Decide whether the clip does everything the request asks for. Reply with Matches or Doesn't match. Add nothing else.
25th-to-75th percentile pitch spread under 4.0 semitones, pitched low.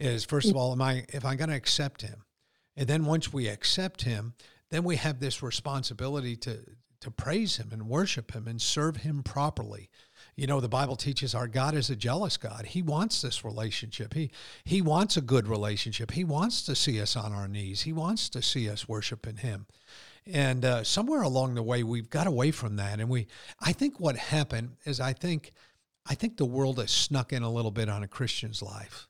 Doesn't match